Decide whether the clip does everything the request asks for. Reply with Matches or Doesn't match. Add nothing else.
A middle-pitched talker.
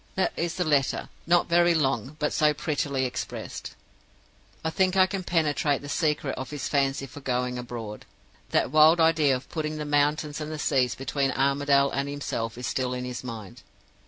Matches